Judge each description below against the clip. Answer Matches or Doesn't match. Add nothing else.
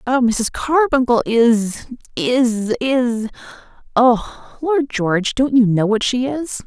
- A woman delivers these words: Matches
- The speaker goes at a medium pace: Doesn't match